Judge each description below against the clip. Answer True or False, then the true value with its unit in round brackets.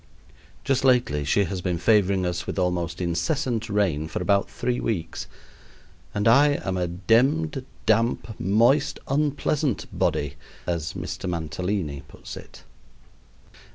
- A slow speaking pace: True (125 wpm)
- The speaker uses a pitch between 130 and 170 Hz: False (100 Hz)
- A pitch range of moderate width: False (6.1 semitones)